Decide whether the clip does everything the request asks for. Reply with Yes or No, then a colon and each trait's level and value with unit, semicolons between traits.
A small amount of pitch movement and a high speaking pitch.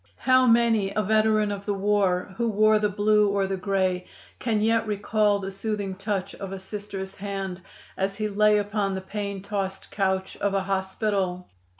Yes: narrow, 1.6 semitones; high, 200 Hz